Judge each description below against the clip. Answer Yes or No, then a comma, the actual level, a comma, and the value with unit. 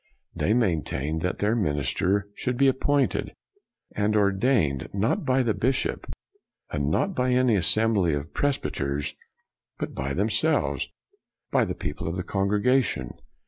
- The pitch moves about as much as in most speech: No, wide, 8.2 semitones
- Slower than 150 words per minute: Yes, average, 140 wpm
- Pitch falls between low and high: No, low, 100 Hz